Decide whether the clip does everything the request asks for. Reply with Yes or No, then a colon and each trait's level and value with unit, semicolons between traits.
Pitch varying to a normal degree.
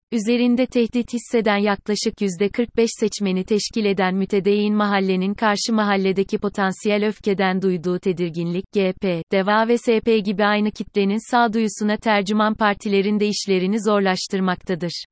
No: narrow, 2.3 semitones